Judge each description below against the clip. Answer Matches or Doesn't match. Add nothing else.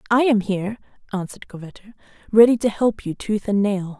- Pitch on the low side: Doesn't match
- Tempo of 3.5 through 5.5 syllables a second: Doesn't match